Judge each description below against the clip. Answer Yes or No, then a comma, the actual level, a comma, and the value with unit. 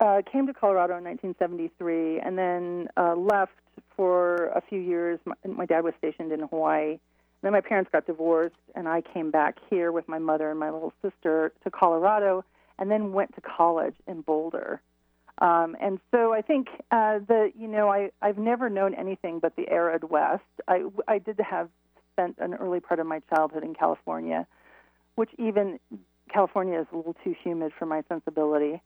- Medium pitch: Yes, medium, 175 Hz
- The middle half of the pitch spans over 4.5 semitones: No, average, 3.8 semitones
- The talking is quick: No, average, 185 wpm